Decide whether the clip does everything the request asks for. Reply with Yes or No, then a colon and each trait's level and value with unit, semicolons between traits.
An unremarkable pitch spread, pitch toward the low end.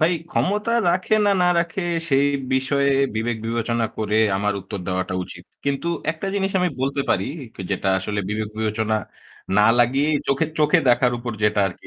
No: wide, 6.1 semitones; low, 120 Hz